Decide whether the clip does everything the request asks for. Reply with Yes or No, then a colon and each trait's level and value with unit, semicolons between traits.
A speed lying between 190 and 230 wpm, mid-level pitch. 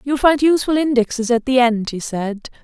No: fast, 205 wpm; very high, 255 Hz